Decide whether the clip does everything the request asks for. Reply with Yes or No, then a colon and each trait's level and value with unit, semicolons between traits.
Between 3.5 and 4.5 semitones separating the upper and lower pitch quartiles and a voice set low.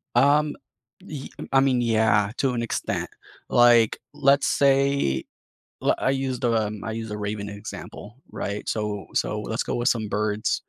Yes: average, 4.1 semitones; low, 115 Hz